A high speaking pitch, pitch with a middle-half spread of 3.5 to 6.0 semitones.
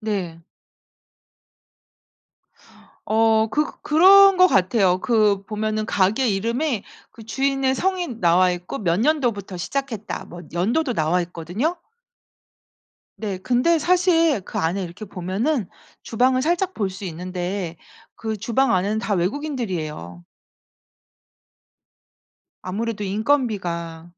No: high, 215 Hz; wide, 6.5 semitones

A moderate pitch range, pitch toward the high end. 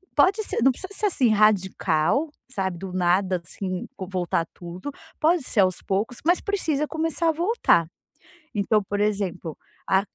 No: wide, 8.9 semitones; high, 205 Hz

